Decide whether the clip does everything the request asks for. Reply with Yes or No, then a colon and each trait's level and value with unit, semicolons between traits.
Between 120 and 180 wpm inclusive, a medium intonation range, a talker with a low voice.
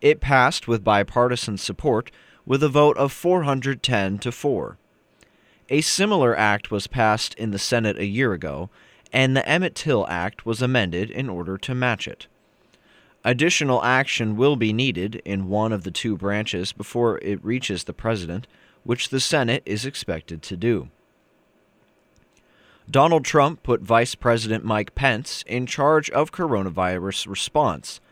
Yes: average, 145 wpm; average, 4.8 semitones; low, 115 Hz